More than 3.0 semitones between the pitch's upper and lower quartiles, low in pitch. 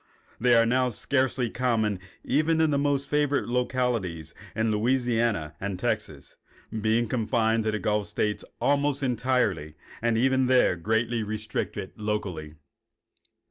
Yes: average, 3.4 semitones; low, 115 Hz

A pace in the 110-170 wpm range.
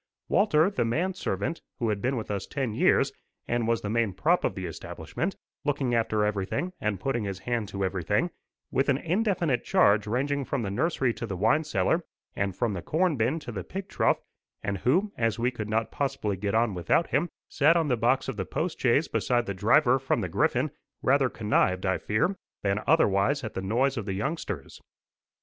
No: fast, 205 wpm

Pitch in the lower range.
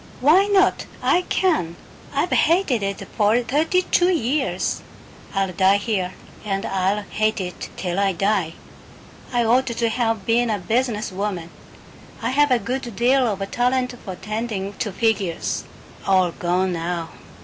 No: high, 215 Hz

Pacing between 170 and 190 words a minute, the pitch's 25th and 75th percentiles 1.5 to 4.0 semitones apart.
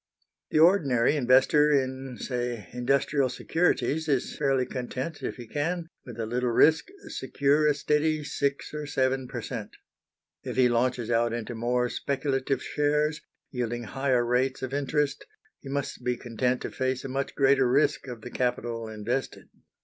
No: average, 155 wpm; average, 2.8 semitones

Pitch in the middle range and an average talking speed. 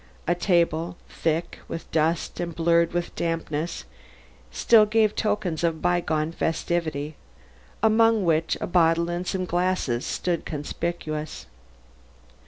No: medium, 170 Hz; slow, 120 wpm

